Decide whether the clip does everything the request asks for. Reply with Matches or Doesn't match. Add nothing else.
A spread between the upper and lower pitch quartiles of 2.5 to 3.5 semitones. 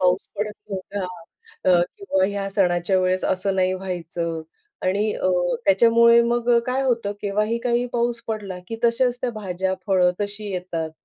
Doesn't match